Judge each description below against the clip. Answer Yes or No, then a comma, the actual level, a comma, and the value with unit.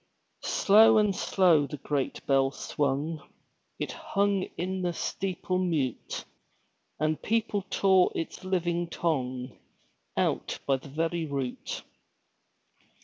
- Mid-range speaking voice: Yes, medium, 170 Hz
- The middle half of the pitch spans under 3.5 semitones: No, average, 5.0 semitones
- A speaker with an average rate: No, slow, 110 wpm